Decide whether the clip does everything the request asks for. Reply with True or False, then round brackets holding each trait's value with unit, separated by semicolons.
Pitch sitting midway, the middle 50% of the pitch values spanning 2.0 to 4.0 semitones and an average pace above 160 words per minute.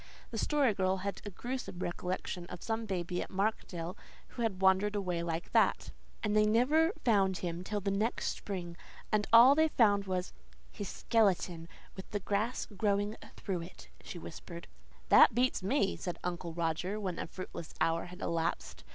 False (195 Hz; 3.3 semitones; 170 wpm)